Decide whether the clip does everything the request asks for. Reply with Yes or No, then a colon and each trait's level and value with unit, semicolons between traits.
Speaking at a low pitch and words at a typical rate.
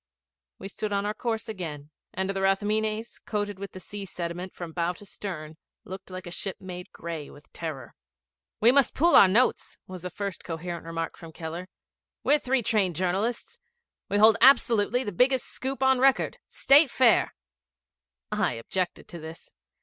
No: high, 195 Hz; average, 170 wpm